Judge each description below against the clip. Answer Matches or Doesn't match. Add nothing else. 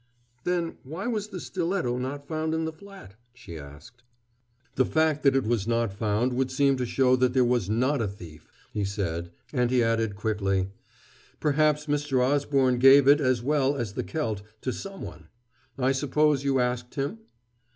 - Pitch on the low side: Matches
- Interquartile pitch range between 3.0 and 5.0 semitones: Matches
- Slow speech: Doesn't match